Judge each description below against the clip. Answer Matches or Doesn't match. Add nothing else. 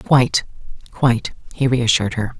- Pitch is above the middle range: Doesn't match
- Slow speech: Matches